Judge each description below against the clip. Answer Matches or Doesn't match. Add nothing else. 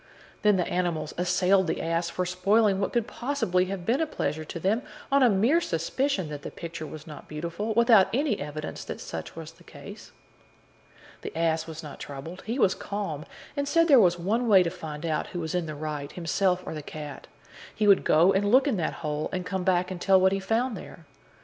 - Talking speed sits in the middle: Doesn't match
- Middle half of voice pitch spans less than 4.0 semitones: Doesn't match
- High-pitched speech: Doesn't match